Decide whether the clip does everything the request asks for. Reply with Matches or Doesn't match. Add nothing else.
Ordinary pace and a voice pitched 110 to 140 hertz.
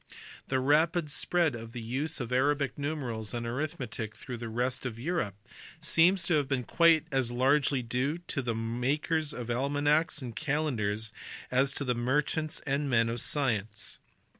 Matches